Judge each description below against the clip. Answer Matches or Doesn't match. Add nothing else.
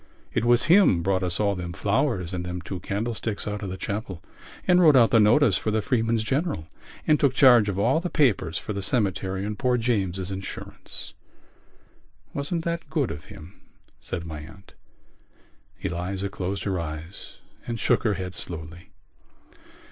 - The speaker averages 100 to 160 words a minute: Doesn't match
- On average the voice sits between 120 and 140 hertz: Doesn't match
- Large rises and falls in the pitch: Doesn't match